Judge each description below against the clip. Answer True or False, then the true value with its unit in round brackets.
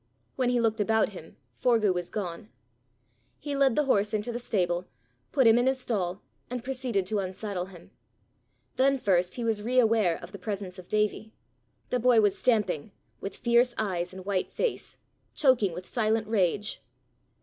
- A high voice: True (215 Hz)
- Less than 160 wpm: False (170 wpm)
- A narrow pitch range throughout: False (4.4 semitones)